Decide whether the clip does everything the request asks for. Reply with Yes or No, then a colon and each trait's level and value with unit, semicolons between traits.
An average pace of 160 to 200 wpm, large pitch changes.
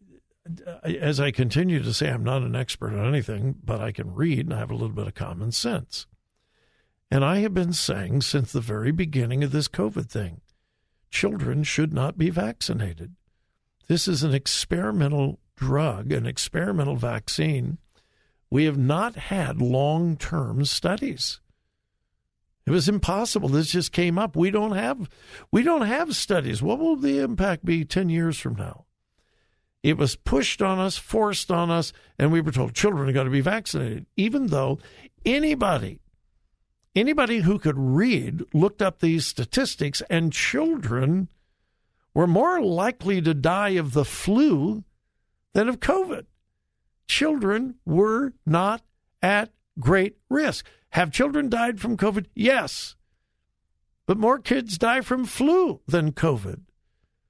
No: average, 150 wpm; wide, 7.0 semitones